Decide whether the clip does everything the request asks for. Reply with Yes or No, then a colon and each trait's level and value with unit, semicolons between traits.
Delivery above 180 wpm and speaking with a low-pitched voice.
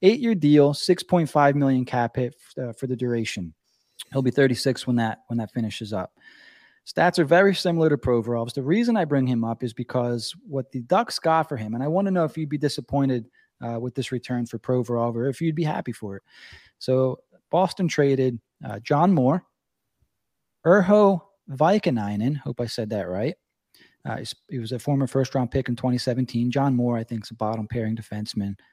Yes: average, 200 wpm; low, 130 Hz